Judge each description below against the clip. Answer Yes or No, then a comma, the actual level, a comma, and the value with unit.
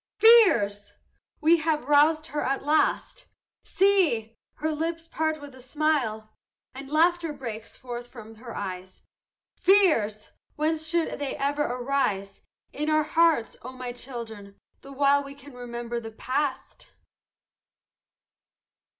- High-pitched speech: Yes, very high, 275 Hz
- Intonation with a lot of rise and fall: No, average, 5.0 semitones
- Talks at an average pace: No, slow, 125 wpm